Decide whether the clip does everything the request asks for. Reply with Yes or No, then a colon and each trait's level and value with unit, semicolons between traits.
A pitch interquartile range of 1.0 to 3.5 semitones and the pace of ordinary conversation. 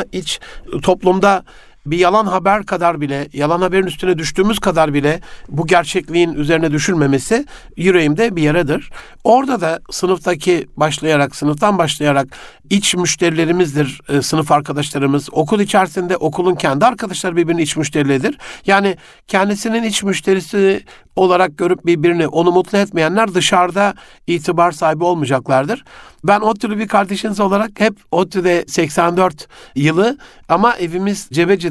No: average, 3.9 semitones; average, 125 wpm